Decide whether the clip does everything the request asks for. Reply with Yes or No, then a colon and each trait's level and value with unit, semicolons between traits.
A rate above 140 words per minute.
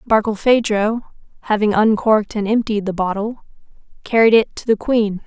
No: slow, 135 wpm